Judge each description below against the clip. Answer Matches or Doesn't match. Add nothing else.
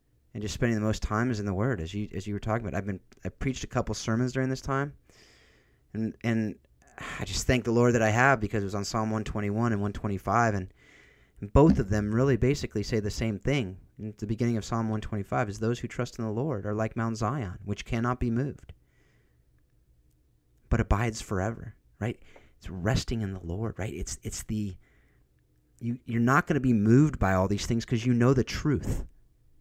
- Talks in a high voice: Doesn't match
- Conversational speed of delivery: Doesn't match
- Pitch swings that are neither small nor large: Matches